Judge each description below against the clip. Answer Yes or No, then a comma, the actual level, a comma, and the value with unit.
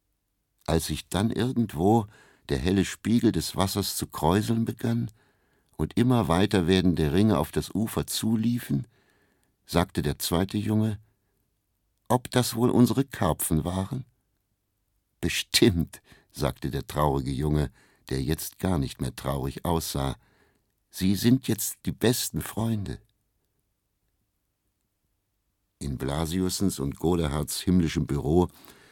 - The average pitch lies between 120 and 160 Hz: No, low, 100 Hz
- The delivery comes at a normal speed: No, slow, 115 wpm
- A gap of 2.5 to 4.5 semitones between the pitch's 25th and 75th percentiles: No, average, 4.9 semitones